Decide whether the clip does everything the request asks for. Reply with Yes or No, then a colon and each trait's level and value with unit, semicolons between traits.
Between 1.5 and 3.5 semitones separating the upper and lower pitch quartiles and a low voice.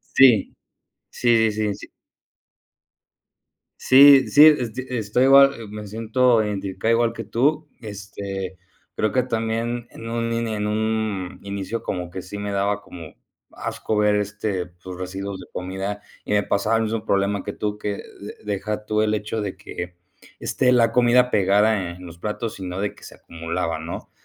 Yes: average, 2.8 semitones; low, 105 Hz